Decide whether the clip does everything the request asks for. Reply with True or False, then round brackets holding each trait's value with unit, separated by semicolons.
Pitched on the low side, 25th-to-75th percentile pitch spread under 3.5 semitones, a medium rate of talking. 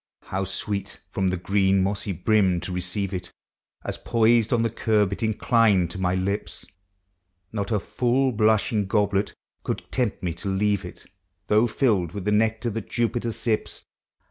True (105 Hz; 2.7 semitones; 165 wpm)